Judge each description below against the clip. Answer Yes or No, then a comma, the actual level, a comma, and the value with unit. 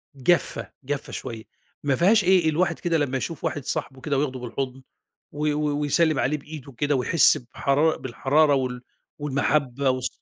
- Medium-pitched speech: Yes, medium, 145 Hz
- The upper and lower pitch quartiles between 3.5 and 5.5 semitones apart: No, average, 2.7 semitones